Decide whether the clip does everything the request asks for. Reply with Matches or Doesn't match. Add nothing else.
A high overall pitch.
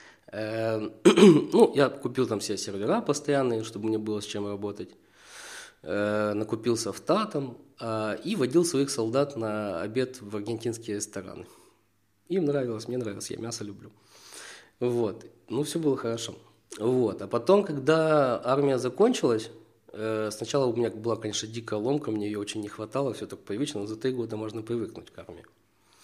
Doesn't match